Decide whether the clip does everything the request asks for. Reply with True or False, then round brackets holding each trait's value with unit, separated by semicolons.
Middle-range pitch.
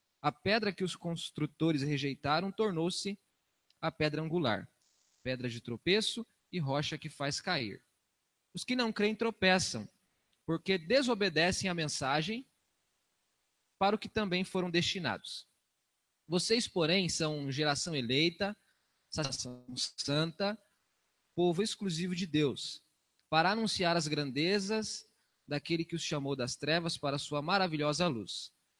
True (165 Hz)